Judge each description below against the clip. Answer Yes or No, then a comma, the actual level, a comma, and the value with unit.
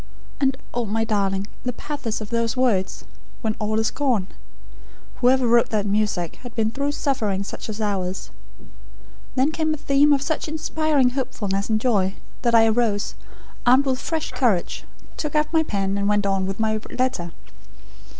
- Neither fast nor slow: Yes, average, 170 wpm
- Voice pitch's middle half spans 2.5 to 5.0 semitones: Yes, average, 4.7 semitones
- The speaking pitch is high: Yes, high, 230 Hz